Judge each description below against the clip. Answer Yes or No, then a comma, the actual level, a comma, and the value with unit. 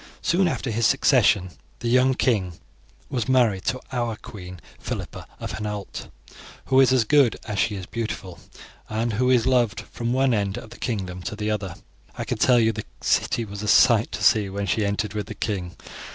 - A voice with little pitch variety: No, average, 3.3 semitones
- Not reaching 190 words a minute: No, average, 195 wpm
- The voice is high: No, low, 110 Hz